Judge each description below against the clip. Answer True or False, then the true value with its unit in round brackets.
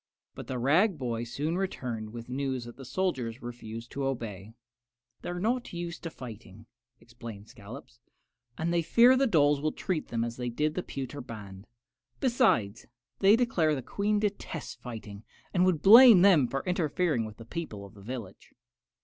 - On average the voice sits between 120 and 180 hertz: True (135 Hz)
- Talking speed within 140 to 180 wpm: True (175 wpm)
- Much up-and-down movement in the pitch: True (7.3 semitones)